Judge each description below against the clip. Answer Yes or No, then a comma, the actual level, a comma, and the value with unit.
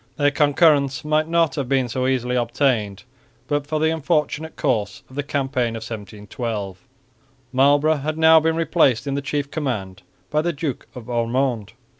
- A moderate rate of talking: Yes, average, 165 wpm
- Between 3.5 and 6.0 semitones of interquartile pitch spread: Yes, average, 4.3 semitones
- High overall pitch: No, medium, 140 Hz